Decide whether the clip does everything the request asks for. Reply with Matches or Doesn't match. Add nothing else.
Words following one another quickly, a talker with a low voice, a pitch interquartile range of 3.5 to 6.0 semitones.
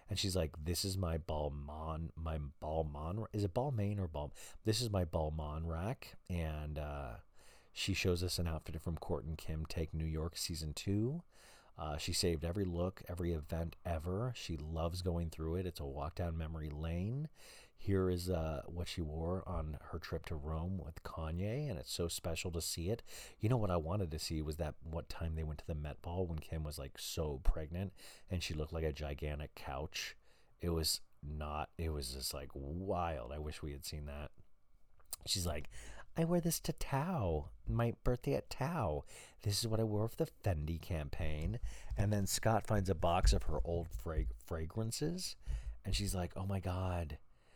Doesn't match